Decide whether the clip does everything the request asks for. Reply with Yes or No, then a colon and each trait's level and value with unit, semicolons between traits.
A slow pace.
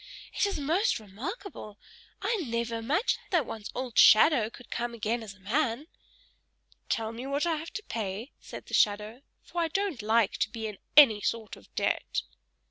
No: average, 180 wpm